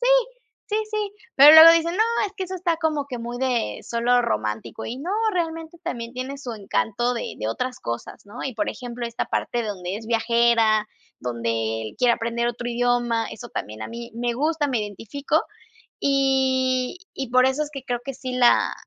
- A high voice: Yes, high, 245 Hz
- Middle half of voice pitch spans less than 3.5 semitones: No, average, 3.9 semitones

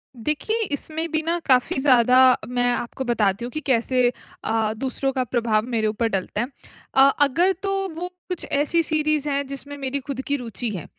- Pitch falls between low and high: No, very high, 260 Hz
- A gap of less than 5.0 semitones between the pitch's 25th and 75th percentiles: Yes, average, 3.8 semitones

